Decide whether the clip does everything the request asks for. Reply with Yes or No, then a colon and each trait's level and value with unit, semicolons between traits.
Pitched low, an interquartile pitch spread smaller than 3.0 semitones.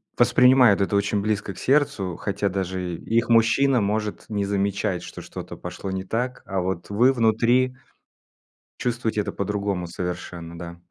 No: low, 100 Hz; average, 3.6 semitones